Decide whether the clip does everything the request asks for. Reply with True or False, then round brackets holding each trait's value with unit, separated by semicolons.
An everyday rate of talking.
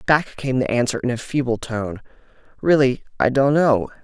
True (180 wpm)